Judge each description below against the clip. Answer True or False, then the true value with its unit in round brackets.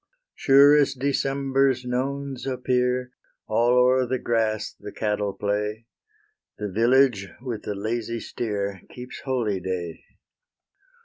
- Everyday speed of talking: False (110 wpm)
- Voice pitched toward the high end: False (125 Hz)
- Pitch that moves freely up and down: False (3.9 semitones)